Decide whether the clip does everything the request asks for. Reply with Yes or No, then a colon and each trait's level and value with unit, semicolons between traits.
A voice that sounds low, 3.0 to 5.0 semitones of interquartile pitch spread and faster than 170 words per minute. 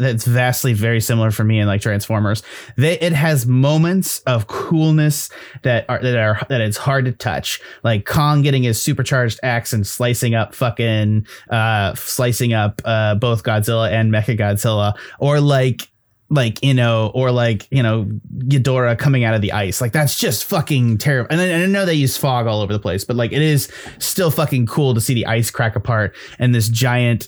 Yes: low, 120 Hz; average, 3.5 semitones; average, 200 wpm